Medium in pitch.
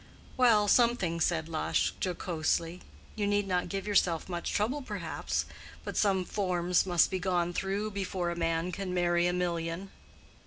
Yes: medium, 180 Hz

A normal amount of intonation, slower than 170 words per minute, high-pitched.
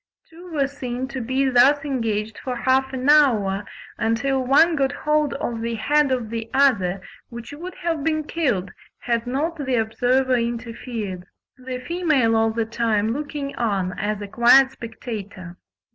Yes: average, 3.8 semitones; average, 160 wpm; very high, 250 Hz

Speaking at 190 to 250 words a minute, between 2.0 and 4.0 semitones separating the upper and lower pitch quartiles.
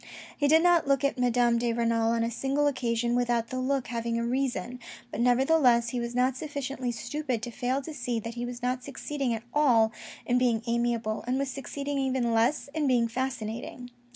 Yes: average, 200 wpm; narrow, 2.5 semitones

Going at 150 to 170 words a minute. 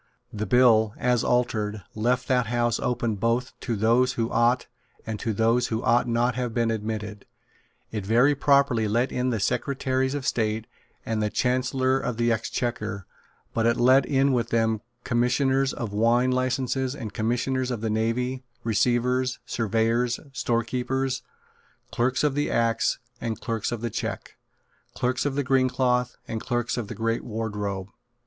Yes: average, 160 wpm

